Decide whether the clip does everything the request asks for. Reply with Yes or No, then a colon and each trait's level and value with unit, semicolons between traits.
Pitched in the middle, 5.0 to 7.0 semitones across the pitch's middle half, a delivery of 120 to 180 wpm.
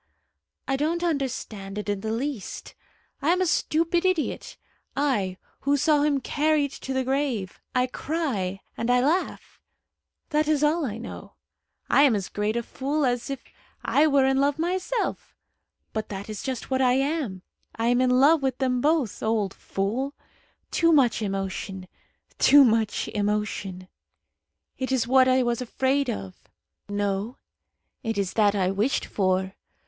No: very high, 255 Hz; wide, 5.5 semitones; average, 160 wpm